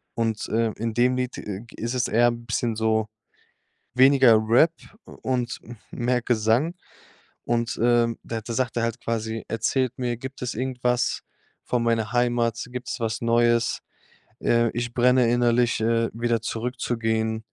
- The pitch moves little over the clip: Yes, narrow, 1.4 semitones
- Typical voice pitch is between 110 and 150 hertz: Yes, low, 120 Hz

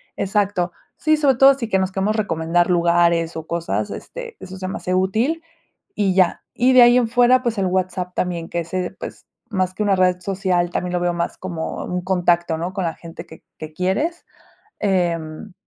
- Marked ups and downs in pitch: No, average, 3.3 semitones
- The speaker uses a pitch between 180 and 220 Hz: Yes, medium, 185 Hz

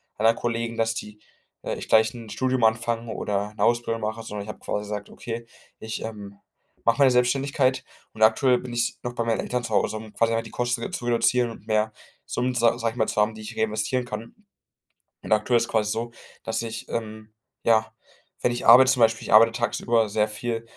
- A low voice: Yes, low, 115 Hz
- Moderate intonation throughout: No, narrow, 1.7 semitones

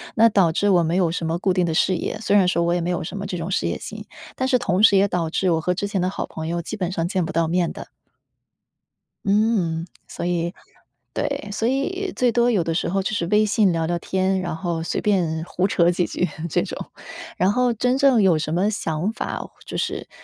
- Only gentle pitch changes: No, average, 3.5 semitones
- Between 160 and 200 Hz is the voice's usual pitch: Yes, medium, 185 Hz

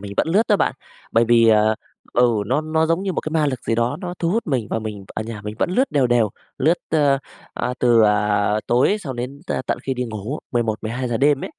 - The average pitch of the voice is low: Yes, low, 125 Hz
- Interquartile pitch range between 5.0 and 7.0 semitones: Yes, wide, 5.6 semitones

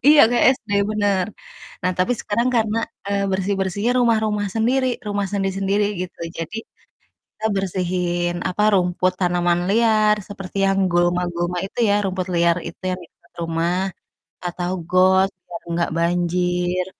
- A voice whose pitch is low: No, medium, 185 Hz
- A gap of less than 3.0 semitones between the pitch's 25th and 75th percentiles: Yes, narrow, 2.6 semitones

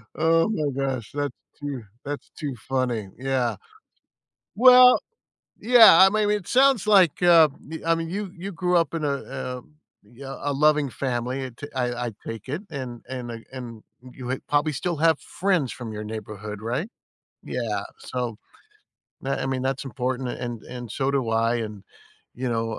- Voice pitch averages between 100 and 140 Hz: Yes, low, 135 Hz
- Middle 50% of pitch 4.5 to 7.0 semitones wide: Yes, average, 5.3 semitones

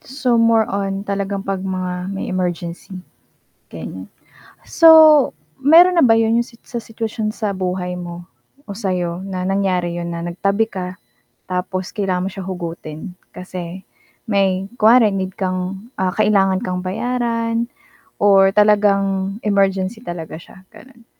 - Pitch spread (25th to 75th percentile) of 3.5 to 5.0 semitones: No, average, 2.9 semitones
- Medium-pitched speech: No, high, 195 Hz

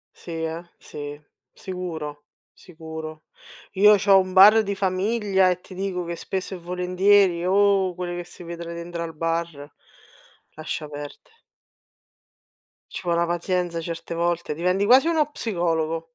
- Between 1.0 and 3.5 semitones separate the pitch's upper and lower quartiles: Yes, narrow, 2.6 semitones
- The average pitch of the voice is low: No, medium, 175 Hz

